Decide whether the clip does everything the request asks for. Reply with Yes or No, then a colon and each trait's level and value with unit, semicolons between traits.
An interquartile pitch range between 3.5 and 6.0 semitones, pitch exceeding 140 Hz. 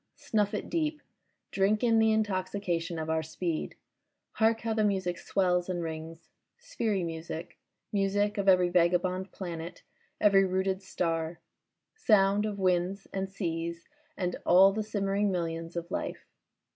No: average, 3.0 semitones; medium, 185 Hz